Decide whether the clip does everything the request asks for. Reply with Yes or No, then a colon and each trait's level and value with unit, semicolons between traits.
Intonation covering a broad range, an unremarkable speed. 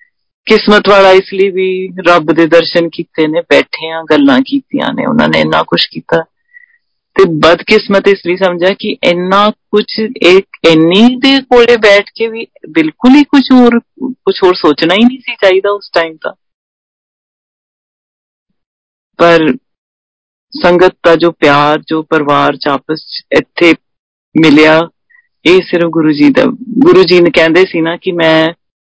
Yes: wide, 6.3 semitones; average, 150 wpm